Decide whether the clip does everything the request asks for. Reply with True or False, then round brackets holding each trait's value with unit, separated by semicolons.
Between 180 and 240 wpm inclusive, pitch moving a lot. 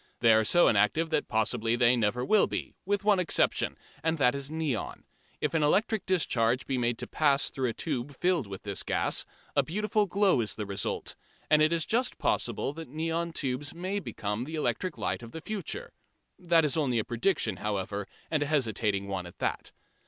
True (195 wpm; 6.7 semitones)